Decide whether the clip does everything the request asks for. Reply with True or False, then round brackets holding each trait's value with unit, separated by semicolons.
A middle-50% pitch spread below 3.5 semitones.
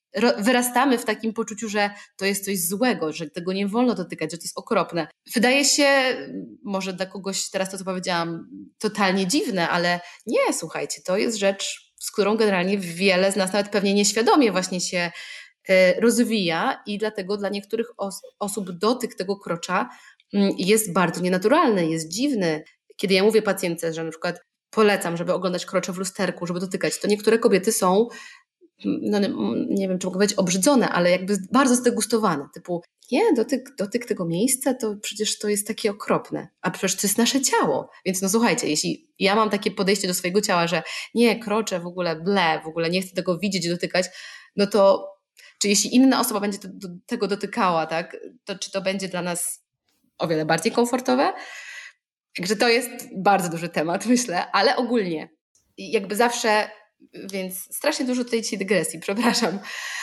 False (3.9 semitones)